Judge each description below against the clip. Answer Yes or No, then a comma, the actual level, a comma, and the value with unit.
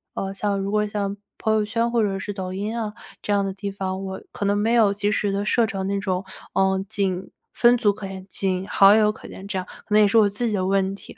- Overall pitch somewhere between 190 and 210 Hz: Yes, high, 200 Hz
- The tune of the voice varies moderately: No, narrow, 1.5 semitones